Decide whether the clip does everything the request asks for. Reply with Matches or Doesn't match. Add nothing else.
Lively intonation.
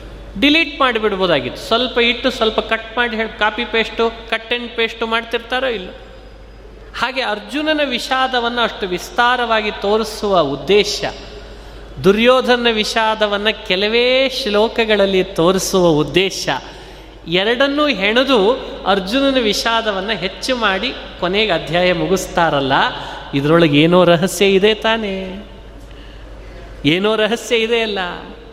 Doesn't match